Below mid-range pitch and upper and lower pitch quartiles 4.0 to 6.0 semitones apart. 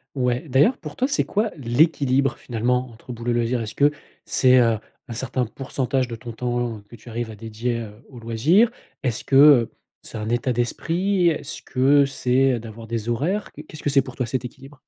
No: low, 125 Hz; average, 3.2 semitones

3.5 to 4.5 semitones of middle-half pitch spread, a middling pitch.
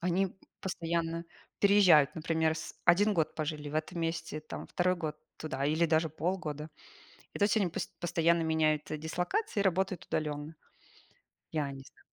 No: narrow, 2.5 semitones; medium, 165 Hz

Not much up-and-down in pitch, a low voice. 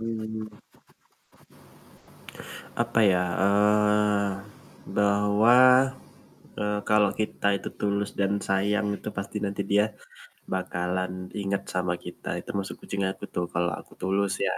Yes: narrow, 1.3 semitones; low, 100 Hz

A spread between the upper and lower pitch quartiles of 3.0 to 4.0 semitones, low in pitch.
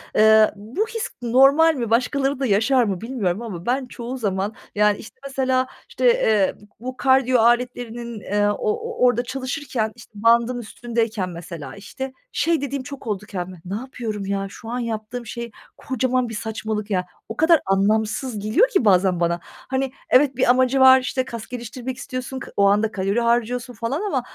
No: average, 3.6 semitones; high, 235 Hz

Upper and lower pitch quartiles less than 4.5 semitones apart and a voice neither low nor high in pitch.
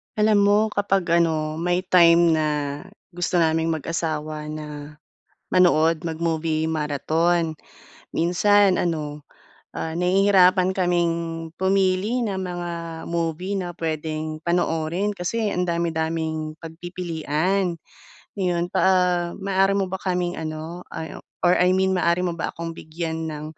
Yes: narrow, 2.6 semitones; medium, 170 Hz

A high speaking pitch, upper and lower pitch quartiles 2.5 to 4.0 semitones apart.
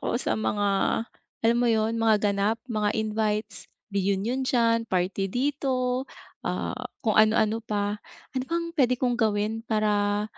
Yes: high, 220 Hz; average, 2.9 semitones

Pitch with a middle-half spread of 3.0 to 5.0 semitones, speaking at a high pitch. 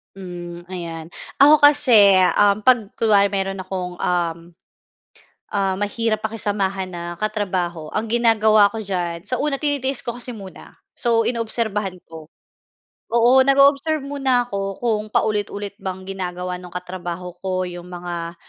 Yes: average, 4.2 semitones; high, 200 Hz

